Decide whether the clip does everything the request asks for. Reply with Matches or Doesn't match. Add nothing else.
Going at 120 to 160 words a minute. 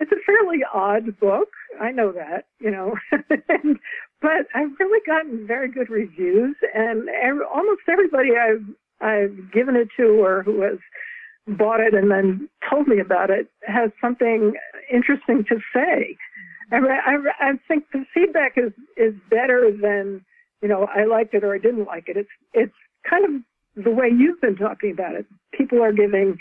Doesn't match